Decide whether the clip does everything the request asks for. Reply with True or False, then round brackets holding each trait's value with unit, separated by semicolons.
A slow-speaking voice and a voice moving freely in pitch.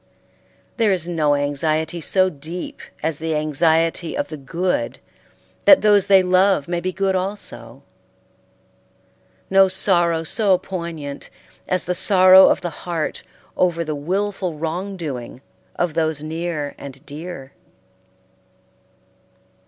False (120 wpm; 3.2 semitones)